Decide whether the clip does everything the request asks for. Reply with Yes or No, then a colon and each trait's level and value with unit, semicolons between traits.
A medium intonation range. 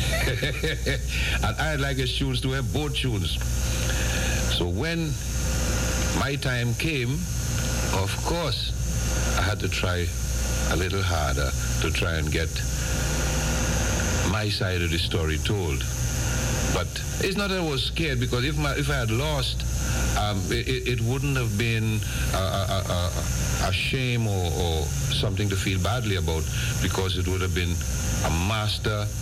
No: wide, 7.8 semitones